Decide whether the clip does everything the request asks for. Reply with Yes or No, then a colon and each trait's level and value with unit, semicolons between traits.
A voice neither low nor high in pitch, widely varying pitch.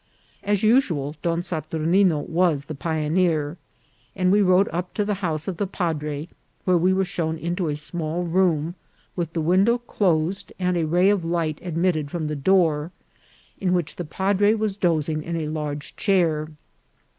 No: medium, 170 Hz; average, 3.2 semitones